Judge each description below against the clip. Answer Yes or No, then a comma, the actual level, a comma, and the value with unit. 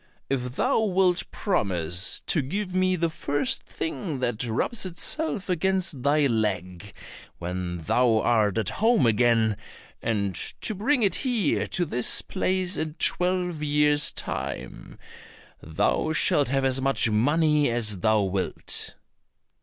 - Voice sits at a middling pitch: Yes, medium, 145 Hz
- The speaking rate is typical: No, slow, 130 wpm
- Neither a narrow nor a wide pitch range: No, wide, 8.9 semitones